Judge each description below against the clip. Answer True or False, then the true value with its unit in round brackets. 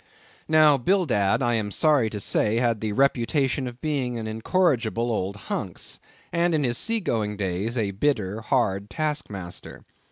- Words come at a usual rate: True (160 wpm)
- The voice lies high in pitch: False (120 Hz)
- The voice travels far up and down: True (5.8 semitones)